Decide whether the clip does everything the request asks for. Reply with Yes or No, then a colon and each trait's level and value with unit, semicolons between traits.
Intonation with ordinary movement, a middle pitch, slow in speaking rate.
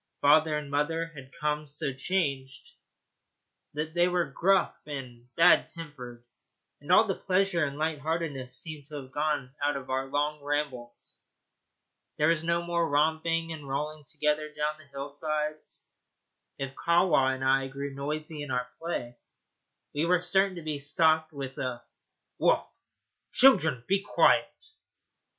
No: average, 3.0 semitones; medium, 150 Hz; average, 145 wpm